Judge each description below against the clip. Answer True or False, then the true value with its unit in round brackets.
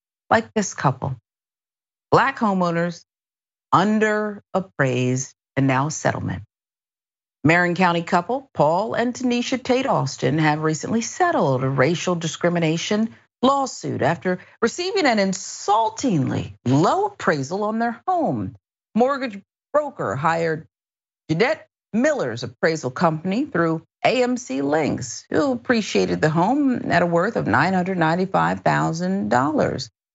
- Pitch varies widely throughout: True (6.9 semitones)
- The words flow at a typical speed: False (105 wpm)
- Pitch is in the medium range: True (180 Hz)